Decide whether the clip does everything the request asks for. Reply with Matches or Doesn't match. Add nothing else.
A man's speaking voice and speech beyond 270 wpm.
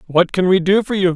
Matches